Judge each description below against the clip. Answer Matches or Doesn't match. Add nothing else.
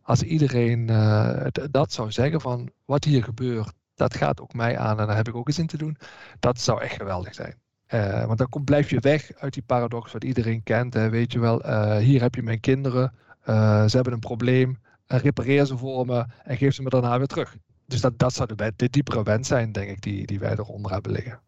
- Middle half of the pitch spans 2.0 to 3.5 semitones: Matches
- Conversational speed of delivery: Doesn't match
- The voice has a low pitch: Matches